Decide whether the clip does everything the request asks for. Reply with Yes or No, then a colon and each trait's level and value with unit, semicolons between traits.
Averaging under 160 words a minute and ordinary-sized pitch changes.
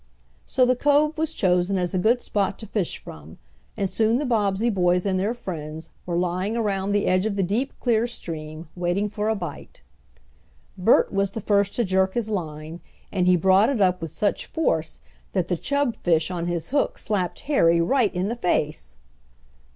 No: average, 190 wpm; average, 4.1 semitones